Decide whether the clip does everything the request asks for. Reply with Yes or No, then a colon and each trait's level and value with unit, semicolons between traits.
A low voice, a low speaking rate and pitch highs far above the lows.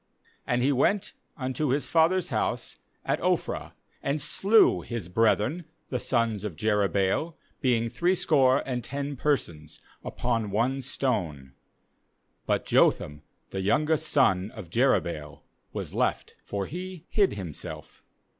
Yes: low, 125 Hz; slow, 125 wpm; wide, 6.8 semitones